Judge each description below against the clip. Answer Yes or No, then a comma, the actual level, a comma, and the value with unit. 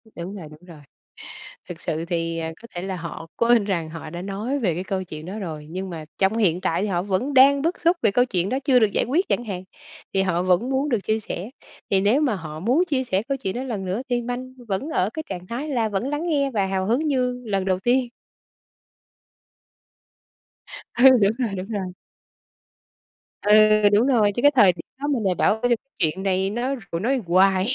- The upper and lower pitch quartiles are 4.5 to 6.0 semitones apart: Yes, wide, 5.4 semitones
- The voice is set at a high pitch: Yes, high, 205 Hz